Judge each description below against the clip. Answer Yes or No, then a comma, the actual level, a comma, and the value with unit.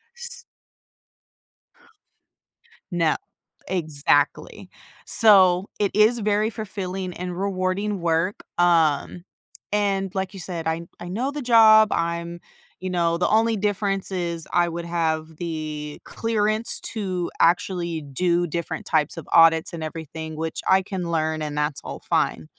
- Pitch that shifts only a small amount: No, average, 3.6 semitones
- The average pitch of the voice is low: No, medium, 175 Hz